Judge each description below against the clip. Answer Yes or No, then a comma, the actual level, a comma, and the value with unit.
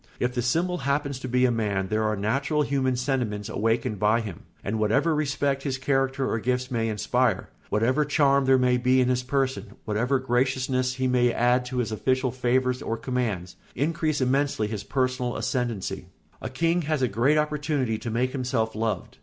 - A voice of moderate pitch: No, low, 125 Hz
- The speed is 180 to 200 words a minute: Yes, average, 185 wpm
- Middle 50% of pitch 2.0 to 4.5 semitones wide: Yes, average, 3.1 semitones